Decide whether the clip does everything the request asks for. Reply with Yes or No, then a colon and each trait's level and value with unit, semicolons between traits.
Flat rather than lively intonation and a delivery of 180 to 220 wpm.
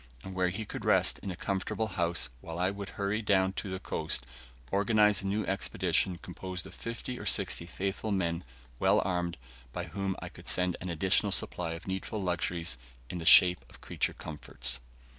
Yes: narrow, 2.3 semitones; average, 185 wpm